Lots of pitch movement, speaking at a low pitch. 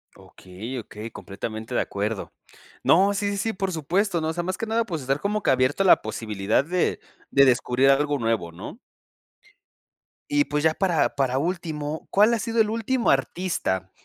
No: wide, 8.6 semitones; medium, 155 Hz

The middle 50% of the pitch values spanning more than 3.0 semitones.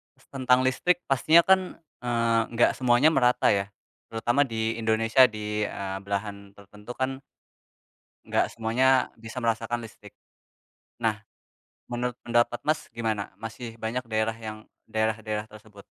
No: narrow, 2.6 semitones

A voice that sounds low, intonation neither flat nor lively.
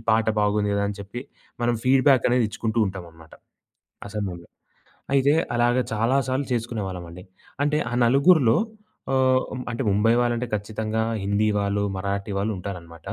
Yes: low, 110 Hz; average, 3.6 semitones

